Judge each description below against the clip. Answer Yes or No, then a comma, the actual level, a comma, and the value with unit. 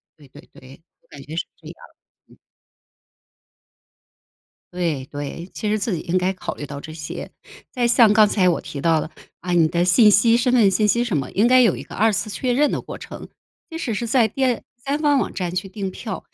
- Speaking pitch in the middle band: No, high, 195 Hz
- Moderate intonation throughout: No, wide, 6.0 semitones